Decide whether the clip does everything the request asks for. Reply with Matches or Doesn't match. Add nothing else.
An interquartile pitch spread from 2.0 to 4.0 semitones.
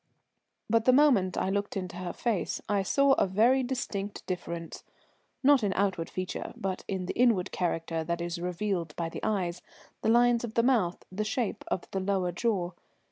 Doesn't match